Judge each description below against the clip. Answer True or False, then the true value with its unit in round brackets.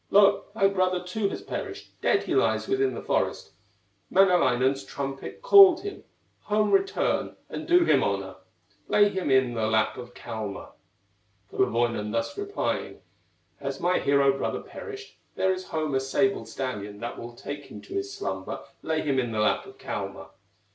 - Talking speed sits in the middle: True (160 wpm)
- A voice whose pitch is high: False (160 Hz)